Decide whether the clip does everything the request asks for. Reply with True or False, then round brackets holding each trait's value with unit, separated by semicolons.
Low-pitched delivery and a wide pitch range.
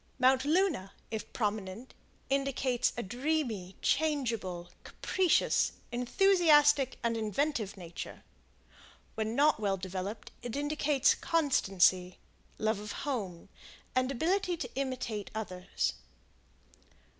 False (245 Hz; 6.3 semitones)